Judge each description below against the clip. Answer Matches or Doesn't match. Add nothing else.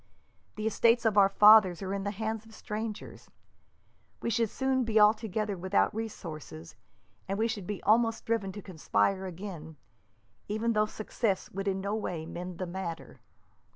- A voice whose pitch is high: Matches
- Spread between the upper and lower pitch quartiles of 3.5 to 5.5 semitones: Doesn't match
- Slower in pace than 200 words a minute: Matches